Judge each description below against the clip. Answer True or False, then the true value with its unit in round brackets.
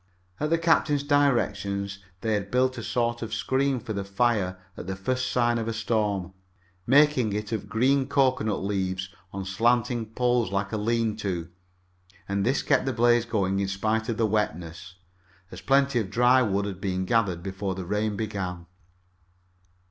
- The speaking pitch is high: False (110 Hz)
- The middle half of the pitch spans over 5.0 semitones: False (3.8 semitones)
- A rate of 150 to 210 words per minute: True (175 wpm)